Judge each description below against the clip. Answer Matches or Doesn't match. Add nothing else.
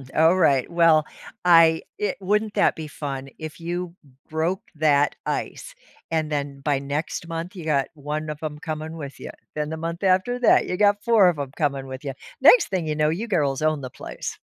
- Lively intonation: Doesn't match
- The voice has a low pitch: Doesn't match